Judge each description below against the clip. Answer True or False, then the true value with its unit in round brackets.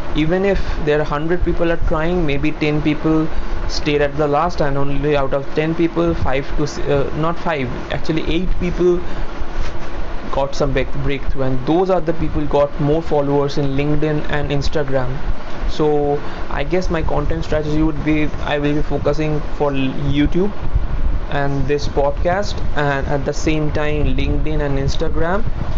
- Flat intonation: True (1.8 semitones)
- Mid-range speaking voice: True (150 Hz)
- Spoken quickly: False (160 wpm)